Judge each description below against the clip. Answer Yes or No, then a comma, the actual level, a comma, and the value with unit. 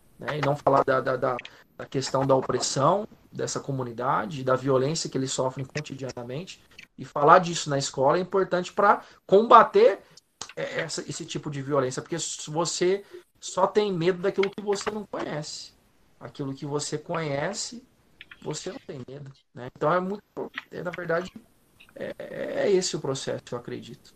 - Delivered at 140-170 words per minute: Yes, average, 160 wpm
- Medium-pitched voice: Yes, medium, 165 Hz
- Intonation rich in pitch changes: Yes, wide, 6.0 semitones